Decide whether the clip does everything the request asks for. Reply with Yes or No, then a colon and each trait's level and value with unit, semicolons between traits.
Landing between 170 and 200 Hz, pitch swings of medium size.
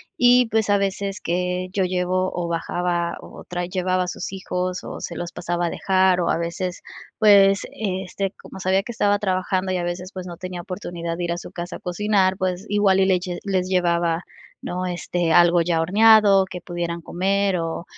No: medium, 185 Hz; narrow, 1.8 semitones